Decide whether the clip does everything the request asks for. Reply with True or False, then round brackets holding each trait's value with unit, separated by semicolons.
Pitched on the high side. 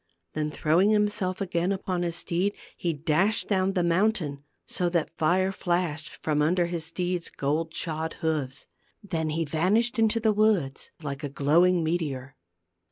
False (170 Hz)